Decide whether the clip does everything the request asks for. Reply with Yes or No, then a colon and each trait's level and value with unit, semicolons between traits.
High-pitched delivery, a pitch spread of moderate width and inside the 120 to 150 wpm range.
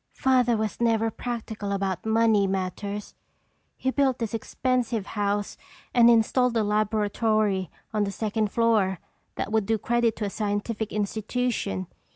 No: high, 220 Hz; narrow, 2.2 semitones; average, 140 wpm